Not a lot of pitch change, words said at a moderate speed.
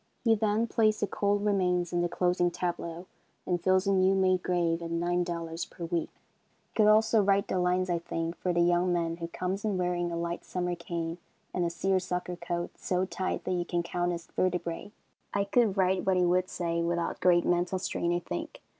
No: narrow, 1.6 semitones; fast, 210 wpm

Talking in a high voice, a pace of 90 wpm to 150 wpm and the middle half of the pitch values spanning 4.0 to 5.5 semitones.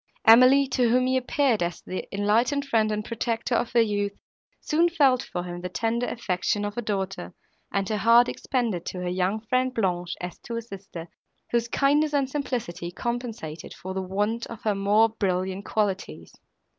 No: high, 220 Hz; average, 175 wpm; average, 4.5 semitones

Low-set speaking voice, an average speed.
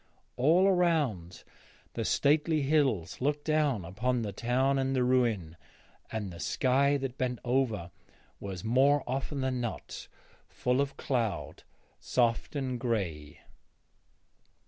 No: low, 125 Hz; slow, 125 wpm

